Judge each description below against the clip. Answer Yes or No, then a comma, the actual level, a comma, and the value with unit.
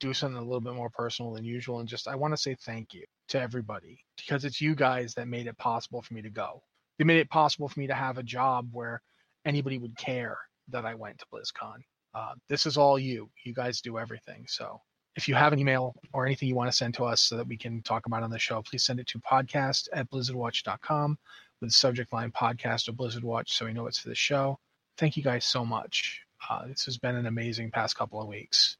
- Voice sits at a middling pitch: No, low, 125 Hz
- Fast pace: Yes, fast, 245 wpm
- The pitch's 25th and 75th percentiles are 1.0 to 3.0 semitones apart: Yes, average, 2.7 semitones